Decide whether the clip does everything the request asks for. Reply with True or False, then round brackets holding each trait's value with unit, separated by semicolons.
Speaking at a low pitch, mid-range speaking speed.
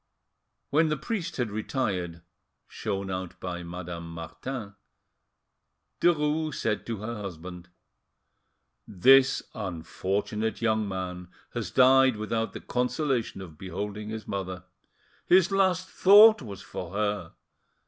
False (105 Hz; 115 wpm)